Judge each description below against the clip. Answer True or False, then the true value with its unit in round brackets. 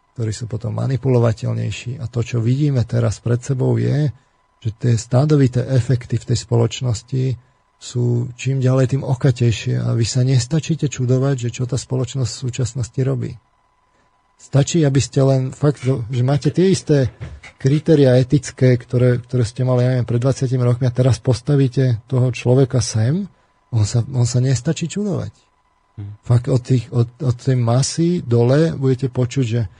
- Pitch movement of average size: False (2.1 semitones)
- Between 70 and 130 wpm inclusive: False (160 wpm)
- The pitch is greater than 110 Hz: True (125 Hz)